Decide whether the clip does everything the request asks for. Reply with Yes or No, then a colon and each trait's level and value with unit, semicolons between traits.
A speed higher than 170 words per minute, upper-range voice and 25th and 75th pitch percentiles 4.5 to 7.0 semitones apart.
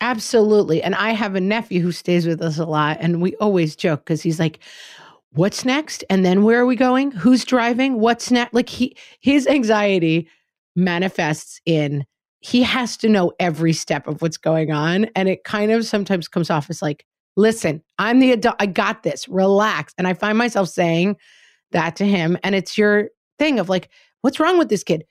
Yes: average, 200 wpm; high, 195 Hz; wide, 5.6 semitones